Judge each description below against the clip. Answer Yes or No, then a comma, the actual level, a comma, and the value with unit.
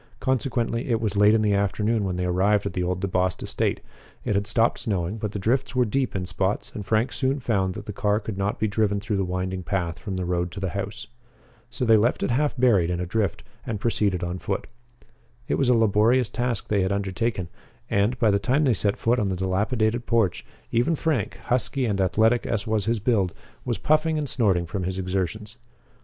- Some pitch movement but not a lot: Yes, average, 3.7 semitones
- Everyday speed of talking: No, fast, 220 wpm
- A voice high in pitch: No, low, 105 Hz